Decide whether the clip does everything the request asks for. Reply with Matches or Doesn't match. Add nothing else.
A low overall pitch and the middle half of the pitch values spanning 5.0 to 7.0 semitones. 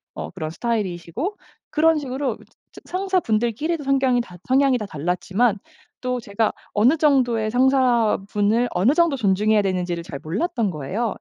Doesn't match